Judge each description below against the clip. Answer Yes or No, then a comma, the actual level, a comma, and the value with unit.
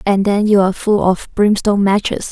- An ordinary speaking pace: Yes, average, 180 wpm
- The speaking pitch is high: Yes, high, 200 Hz